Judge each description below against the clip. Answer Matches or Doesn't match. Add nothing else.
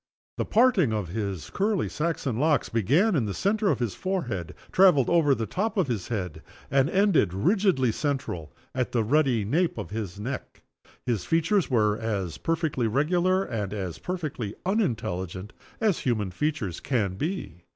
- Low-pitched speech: Matches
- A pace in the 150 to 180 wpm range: Matches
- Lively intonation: Matches